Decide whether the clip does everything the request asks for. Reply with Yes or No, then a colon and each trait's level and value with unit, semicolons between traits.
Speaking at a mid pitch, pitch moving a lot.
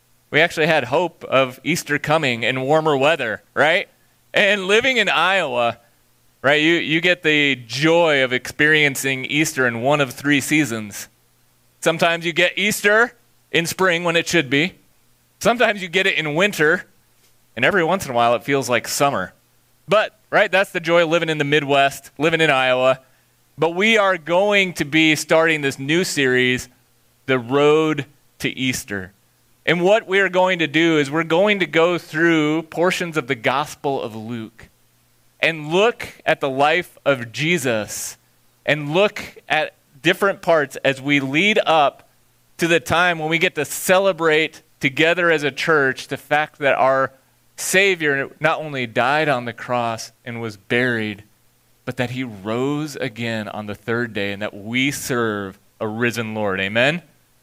Yes: medium, 145 Hz; wide, 5.7 semitones